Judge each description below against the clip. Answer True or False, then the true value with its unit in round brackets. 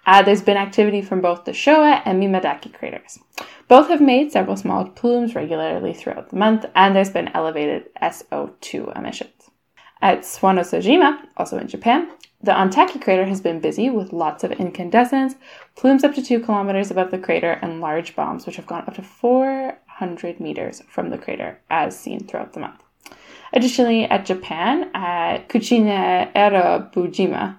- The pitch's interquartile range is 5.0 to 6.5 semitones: True (5.3 semitones)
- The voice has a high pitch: True (200 Hz)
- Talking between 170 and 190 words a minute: False (160 wpm)